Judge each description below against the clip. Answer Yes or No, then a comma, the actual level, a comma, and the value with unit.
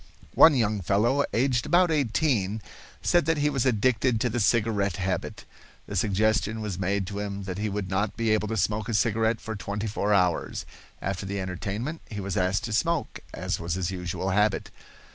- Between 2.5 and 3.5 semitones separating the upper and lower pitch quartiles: Yes, average, 3.0 semitones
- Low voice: Yes, low, 105 Hz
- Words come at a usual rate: Yes, average, 190 wpm